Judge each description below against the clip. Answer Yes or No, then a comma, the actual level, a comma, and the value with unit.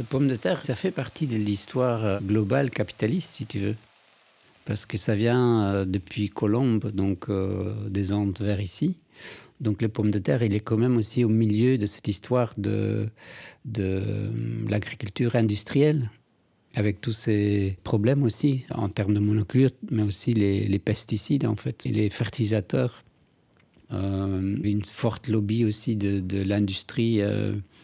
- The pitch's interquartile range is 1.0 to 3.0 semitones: Yes, narrow, 2.6 semitones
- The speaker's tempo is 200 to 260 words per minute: No, average, 155 wpm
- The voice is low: Yes, low, 110 Hz